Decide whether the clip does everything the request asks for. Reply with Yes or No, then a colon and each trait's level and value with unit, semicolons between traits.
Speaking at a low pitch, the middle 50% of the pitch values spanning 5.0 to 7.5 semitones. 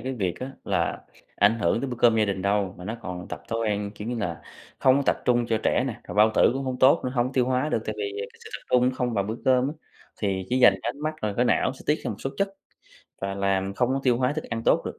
No: low, 115 Hz; average, 4.2 semitones